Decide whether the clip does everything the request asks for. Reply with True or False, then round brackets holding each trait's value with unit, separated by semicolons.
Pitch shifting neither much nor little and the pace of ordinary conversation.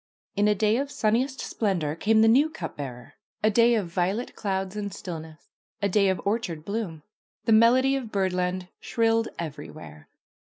True (4.1 semitones; 170 wpm)